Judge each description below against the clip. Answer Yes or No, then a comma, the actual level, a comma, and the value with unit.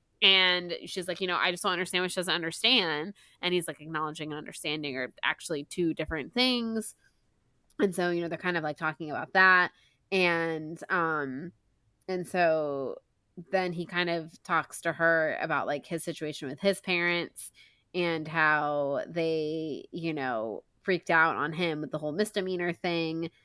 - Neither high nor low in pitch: Yes, medium, 165 Hz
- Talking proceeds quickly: No, average, 170 wpm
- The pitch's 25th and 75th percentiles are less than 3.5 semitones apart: Yes, average, 2.7 semitones